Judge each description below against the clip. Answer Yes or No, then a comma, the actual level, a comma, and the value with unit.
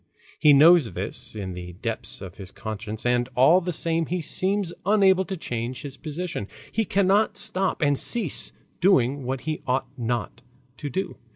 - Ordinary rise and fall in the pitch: No, wide, 7.4 semitones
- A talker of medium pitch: Yes, medium, 145 Hz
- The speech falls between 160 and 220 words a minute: Yes, average, 170 wpm